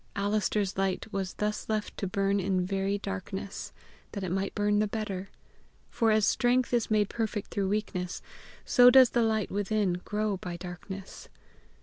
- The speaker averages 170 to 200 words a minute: No, average, 160 wpm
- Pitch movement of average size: No, narrow, 2.0 semitones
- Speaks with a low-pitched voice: No, high, 200 Hz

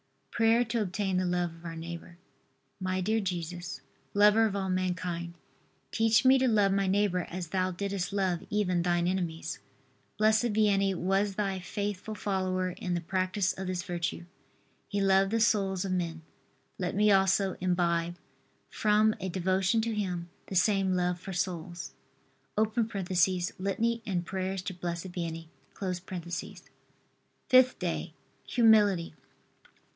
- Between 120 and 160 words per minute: Yes, average, 140 wpm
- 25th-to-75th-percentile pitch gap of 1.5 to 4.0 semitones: Yes, narrow, 2.6 semitones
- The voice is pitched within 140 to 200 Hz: Yes, high, 190 Hz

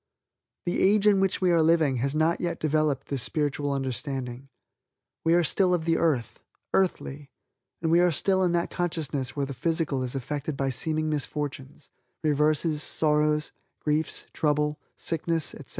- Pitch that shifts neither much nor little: Yes, average, 3.1 semitones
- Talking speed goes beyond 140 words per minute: Yes, average, 160 wpm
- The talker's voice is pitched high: No, medium, 150 Hz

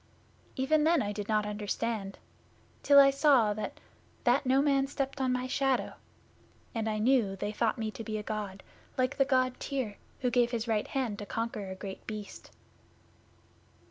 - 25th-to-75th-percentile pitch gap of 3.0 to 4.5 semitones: Yes, average, 4.1 semitones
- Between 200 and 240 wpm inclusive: No, average, 180 wpm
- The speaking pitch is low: No, high, 235 Hz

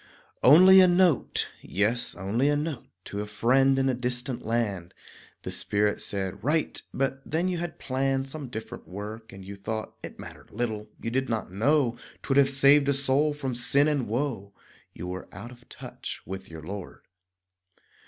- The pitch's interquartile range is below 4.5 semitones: No, average, 5.1 semitones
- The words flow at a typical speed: Yes, average, 175 wpm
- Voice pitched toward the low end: Yes, low, 125 Hz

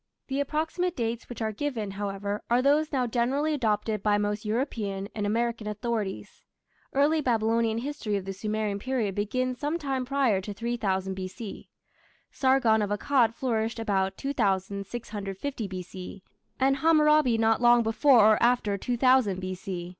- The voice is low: No, high, 225 Hz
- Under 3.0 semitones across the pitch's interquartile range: No, average, 4.2 semitones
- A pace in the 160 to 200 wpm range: No, average, 145 wpm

